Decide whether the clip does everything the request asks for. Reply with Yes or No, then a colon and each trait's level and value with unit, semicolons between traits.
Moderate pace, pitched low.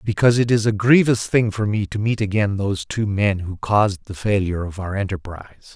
No: fast, 220 wpm; low, 100 Hz